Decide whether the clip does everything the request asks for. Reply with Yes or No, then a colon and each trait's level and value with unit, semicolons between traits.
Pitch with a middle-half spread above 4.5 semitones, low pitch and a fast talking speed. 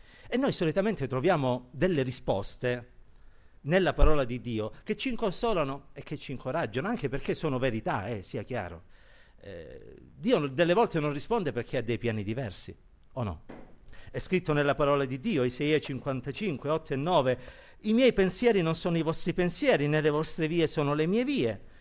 No: wide, 5.6 semitones; medium, 150 Hz; fast, 175 wpm